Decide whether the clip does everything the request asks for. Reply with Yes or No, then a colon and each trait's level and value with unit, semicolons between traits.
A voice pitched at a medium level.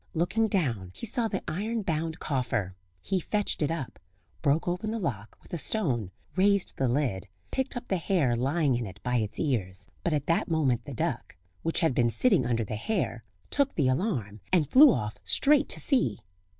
Yes: medium, 155 Hz